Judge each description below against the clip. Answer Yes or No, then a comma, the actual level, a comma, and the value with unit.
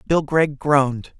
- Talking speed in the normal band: Yes, average, 150 wpm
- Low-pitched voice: No, medium, 145 Hz